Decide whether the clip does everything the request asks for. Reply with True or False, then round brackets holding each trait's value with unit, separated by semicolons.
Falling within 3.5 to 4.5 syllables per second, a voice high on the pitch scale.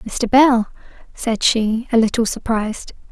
True (4.1 syllables/s; 230 Hz)